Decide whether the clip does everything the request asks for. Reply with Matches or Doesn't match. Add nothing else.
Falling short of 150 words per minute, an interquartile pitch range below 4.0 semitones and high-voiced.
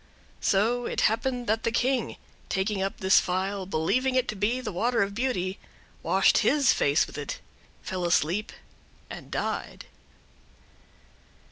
Doesn't match